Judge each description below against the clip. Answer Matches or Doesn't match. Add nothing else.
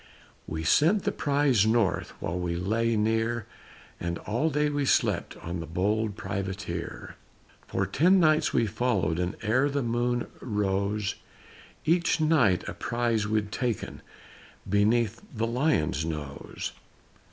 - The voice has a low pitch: Matches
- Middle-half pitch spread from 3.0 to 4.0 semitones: Doesn't match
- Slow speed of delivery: Matches